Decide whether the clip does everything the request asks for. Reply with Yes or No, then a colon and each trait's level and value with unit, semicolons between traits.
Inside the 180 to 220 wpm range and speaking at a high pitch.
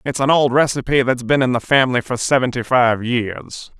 No: fast, 205 wpm; low, 125 Hz